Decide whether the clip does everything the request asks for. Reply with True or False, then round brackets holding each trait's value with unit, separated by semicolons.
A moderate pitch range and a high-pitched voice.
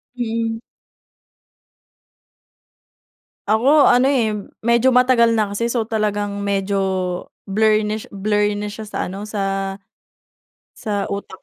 False (2.3 semitones; 210 Hz)